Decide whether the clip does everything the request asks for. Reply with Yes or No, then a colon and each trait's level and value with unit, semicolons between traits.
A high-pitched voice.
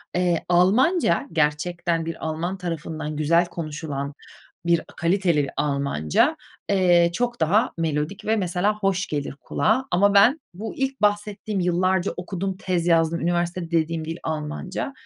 No: medium, 175 Hz